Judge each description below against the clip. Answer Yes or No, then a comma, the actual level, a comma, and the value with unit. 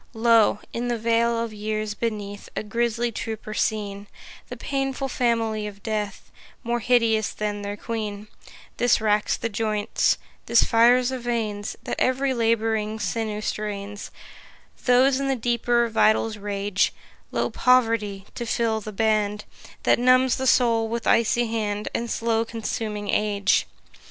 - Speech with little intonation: Yes, narrow, 2.0 semitones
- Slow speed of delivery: No, average, 145 wpm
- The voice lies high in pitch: Yes, high, 225 Hz